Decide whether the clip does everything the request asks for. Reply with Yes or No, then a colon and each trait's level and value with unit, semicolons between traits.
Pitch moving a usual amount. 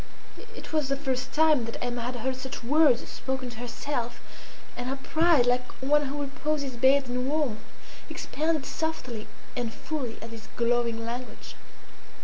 Yes: average, 3.2 semitones